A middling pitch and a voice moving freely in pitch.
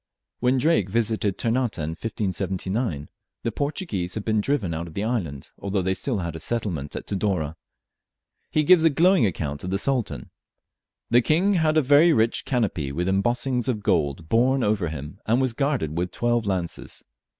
No: low, 110 Hz; wide, 6.5 semitones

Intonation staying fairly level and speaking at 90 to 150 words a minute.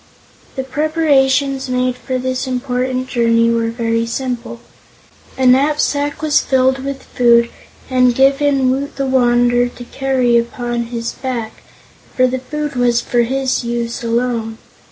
Yes: narrow, 2.1 semitones; slow, 135 wpm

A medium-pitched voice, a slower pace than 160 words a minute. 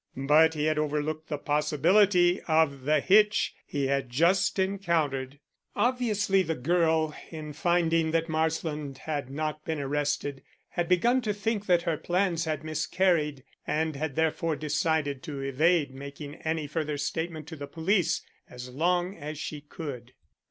Yes: medium, 155 Hz; average, 150 wpm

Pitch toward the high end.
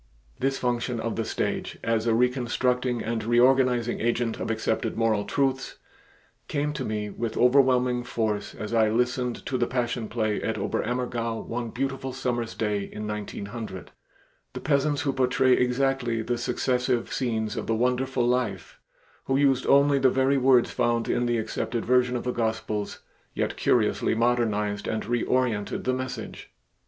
No: low, 120 Hz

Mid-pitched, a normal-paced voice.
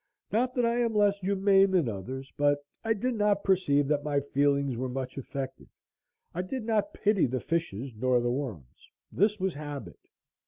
Yes: medium, 145 Hz; average, 180 wpm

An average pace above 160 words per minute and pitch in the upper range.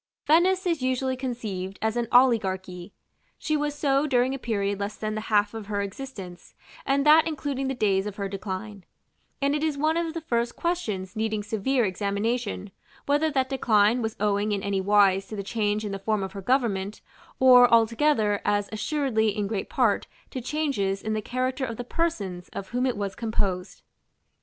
Yes: average, 190 wpm; high, 220 Hz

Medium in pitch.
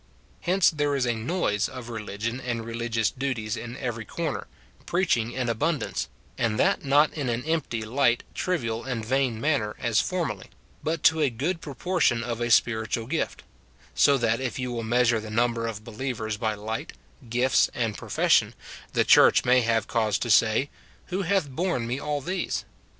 No: low, 120 Hz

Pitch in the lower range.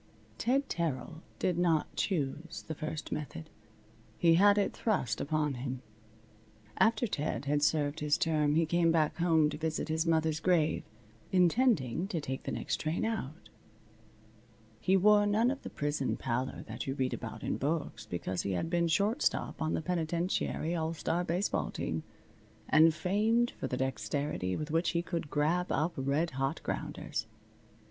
No: medium, 160 Hz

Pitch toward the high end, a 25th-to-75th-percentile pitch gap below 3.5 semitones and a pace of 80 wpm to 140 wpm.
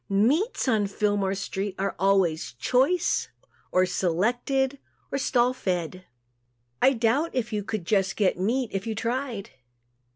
No: high, 210 Hz; average, 4.8 semitones; slow, 135 wpm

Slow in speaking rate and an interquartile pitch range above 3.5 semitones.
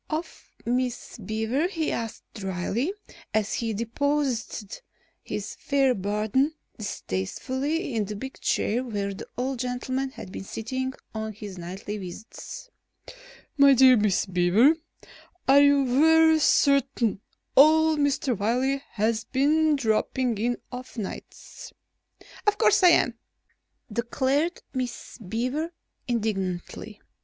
Yes: slow, 115 wpm; average, 4.6 semitones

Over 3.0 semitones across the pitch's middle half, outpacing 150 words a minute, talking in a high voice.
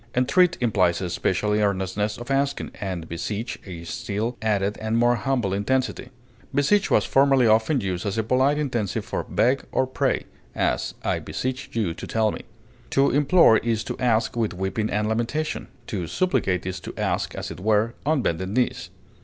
No: average, 4.7 semitones; average, 175 wpm; low, 110 Hz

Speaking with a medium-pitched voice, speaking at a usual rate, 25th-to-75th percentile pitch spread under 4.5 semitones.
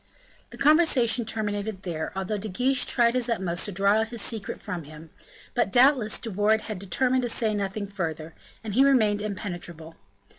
No: high, 210 Hz; average, 180 wpm; average, 3.8 semitones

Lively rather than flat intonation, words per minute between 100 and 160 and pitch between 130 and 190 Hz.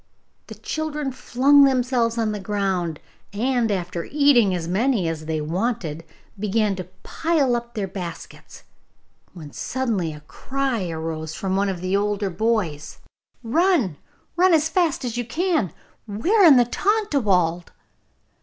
No: wide, 6.9 semitones; average, 145 wpm; high, 215 Hz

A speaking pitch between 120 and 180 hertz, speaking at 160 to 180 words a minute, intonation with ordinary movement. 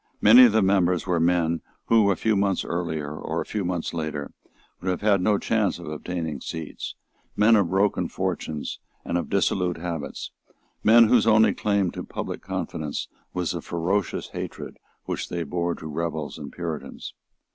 No: very low, 90 Hz; average, 170 wpm; average, 3.6 semitones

